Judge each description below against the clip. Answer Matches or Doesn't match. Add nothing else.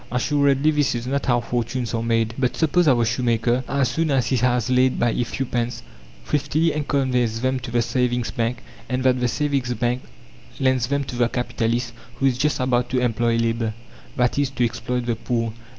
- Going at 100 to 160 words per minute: Doesn't match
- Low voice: Matches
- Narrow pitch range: Matches